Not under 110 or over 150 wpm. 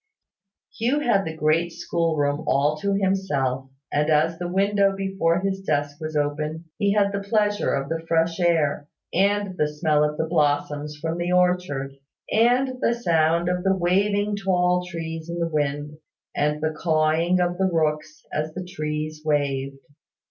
No: average, 170 wpm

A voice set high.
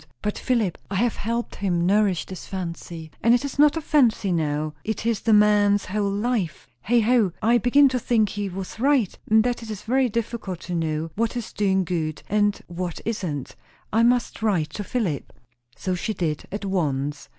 Yes: high, 205 Hz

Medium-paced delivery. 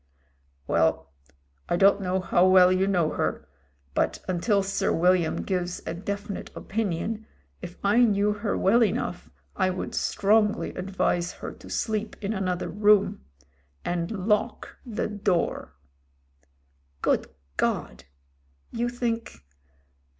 No: slow, 125 wpm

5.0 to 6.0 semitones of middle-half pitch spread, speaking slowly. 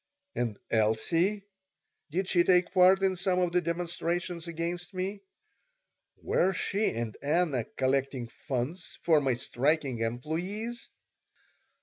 Yes: wide, 5.5 semitones; slow, 115 wpm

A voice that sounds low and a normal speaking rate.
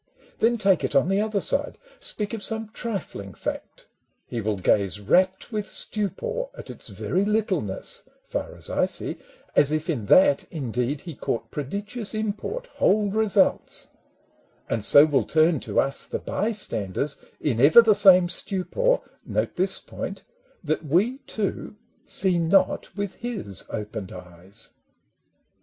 No: medium, 185 Hz; average, 150 wpm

